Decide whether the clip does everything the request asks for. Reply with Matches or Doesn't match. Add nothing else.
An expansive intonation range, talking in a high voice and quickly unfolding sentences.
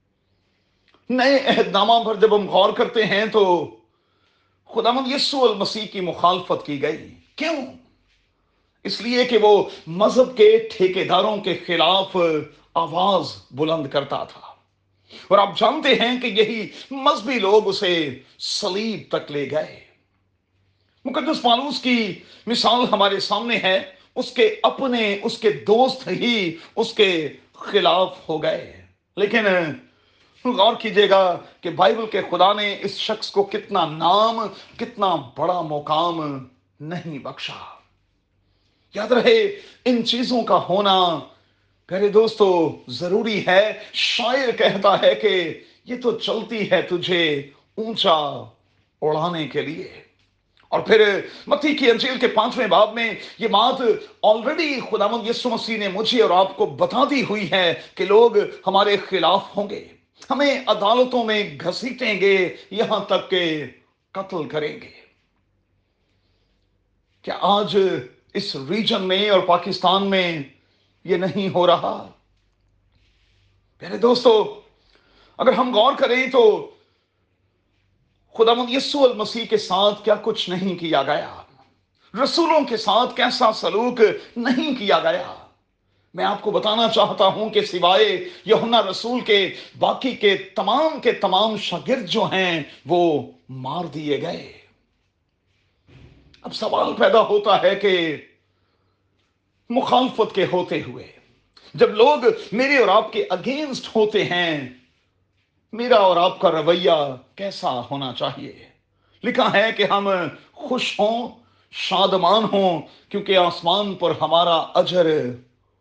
Doesn't match